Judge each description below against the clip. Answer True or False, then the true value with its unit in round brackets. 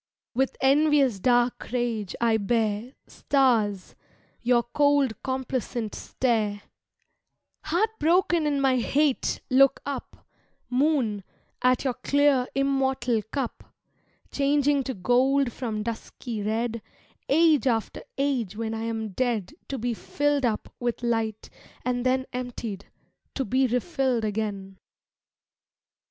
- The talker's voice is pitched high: True (250 Hz)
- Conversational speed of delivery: False (115 wpm)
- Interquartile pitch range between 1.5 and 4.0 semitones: True (3.5 semitones)